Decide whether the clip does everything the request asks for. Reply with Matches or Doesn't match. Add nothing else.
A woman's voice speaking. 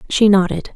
Matches